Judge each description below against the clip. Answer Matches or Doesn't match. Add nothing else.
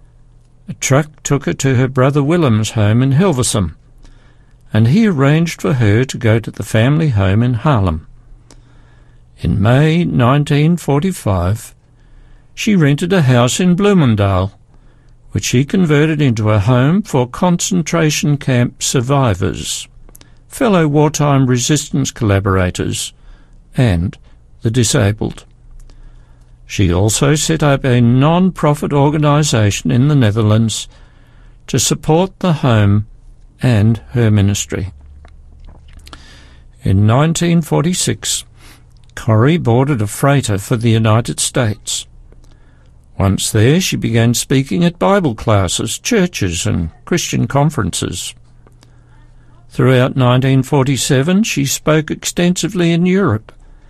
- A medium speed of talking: Doesn't match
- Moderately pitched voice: Doesn't match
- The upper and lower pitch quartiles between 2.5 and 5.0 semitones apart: Doesn't match